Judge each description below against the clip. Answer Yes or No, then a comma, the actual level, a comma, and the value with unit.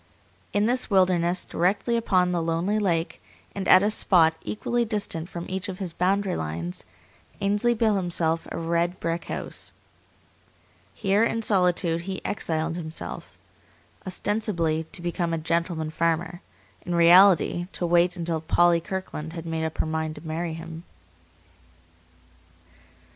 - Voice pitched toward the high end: No, medium, 175 Hz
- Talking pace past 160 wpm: No, average, 140 wpm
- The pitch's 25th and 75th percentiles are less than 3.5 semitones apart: Yes, average, 2.9 semitones